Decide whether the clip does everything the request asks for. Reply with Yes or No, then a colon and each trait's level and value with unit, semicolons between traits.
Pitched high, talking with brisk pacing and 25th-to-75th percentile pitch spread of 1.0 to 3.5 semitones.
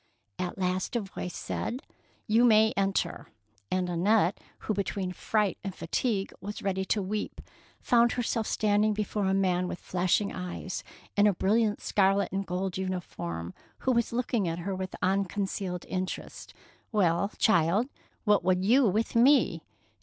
No: high, 195 Hz; average, 160 wpm; average, 2.7 semitones